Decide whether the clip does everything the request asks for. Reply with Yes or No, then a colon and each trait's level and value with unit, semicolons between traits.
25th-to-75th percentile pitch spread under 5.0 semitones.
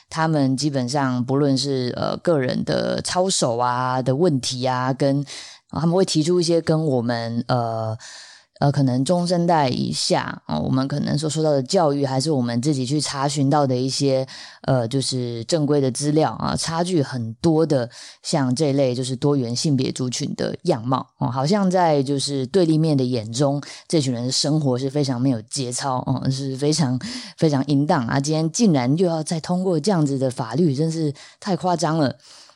Yes: average, 3.6 semitones